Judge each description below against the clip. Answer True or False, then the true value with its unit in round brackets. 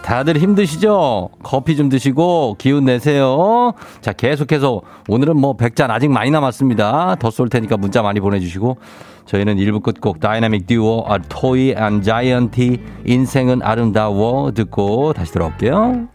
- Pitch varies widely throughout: False (5.0 semitones)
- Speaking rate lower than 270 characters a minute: False (325 characters per minute)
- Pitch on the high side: False (125 Hz)